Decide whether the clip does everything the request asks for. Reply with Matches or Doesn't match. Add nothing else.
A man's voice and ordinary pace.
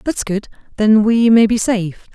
Doesn't match